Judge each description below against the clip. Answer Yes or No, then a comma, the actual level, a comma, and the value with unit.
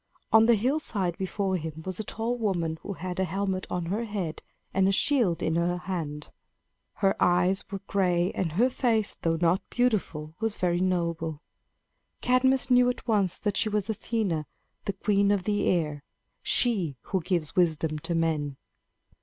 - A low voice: No, medium, 185 Hz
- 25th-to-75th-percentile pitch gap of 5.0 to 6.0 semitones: No, average, 4.2 semitones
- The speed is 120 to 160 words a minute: No, average, 170 wpm